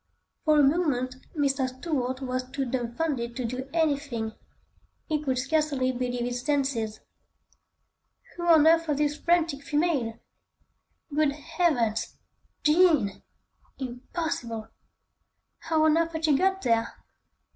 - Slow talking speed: Yes, slow, 120 wpm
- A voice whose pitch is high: Yes, very high, 280 Hz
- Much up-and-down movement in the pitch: No, average, 4.1 semitones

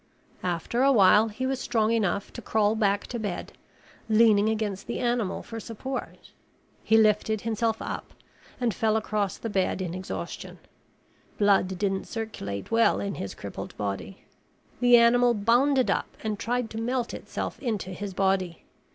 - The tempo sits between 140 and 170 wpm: Yes, average, 155 wpm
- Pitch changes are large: No, average, 2.9 semitones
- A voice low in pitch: No, high, 220 Hz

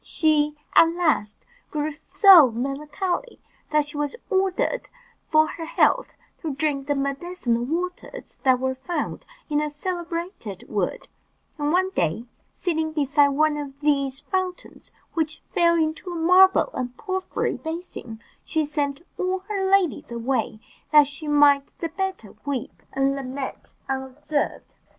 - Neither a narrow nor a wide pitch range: Yes, average, 4.1 semitones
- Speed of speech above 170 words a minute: No, slow, 135 wpm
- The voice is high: Yes, very high, 300 Hz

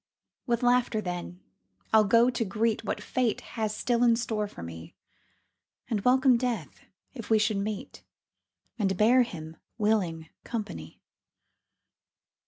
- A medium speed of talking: No, slow, 130 wpm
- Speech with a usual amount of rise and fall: Yes, average, 3.6 semitones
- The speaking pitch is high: Yes, high, 215 Hz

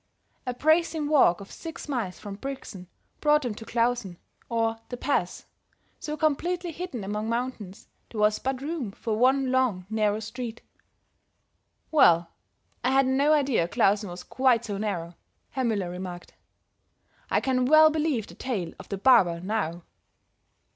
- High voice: Yes, high, 235 Hz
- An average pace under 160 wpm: Yes, average, 150 wpm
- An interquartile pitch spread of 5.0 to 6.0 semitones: Yes, average, 5.3 semitones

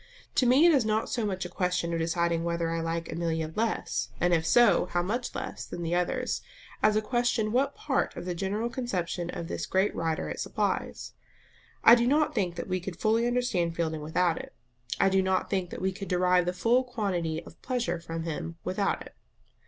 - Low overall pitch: No, medium, 185 Hz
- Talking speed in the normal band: No, fast, 210 wpm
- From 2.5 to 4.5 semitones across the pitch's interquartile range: No, average, 5.0 semitones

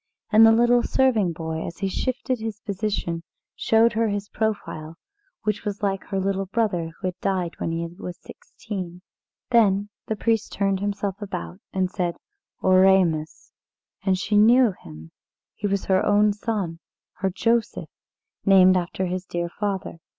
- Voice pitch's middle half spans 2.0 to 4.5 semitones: Yes, average, 2.9 semitones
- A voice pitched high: Yes, high, 195 Hz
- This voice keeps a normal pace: Yes, average, 155 wpm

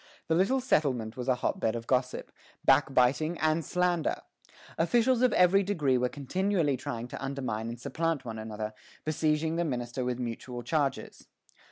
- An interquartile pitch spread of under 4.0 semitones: No, average, 5.3 semitones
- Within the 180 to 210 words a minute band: No, average, 160 wpm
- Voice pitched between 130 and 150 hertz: Yes, medium, 140 Hz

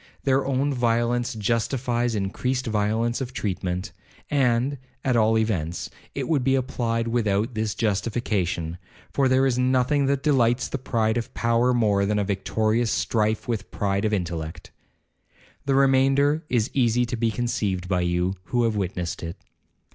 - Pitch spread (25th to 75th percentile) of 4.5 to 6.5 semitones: No, average, 3.6 semitones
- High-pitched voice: No, low, 115 Hz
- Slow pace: No, average, 155 wpm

